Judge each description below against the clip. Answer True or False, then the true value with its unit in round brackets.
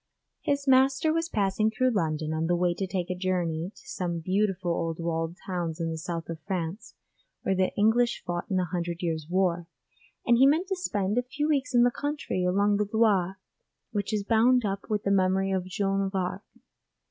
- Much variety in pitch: False (4.2 semitones)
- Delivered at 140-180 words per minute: False (205 wpm)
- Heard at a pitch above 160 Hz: True (190 Hz)